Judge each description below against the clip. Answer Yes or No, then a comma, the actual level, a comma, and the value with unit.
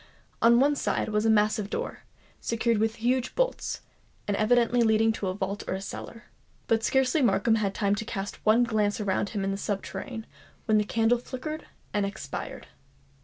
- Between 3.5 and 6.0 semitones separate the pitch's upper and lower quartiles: No, narrow, 2.6 semitones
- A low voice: No, high, 220 Hz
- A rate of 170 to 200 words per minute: Yes, average, 175 wpm